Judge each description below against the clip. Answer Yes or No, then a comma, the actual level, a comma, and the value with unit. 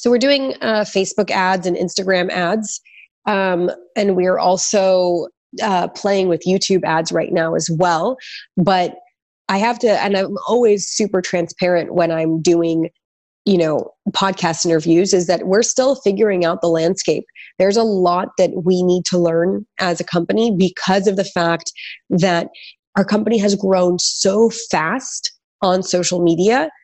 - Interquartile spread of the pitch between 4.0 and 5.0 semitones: No, average, 2.8 semitones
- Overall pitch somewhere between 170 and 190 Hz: Yes, medium, 185 Hz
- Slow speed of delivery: No, average, 160 wpm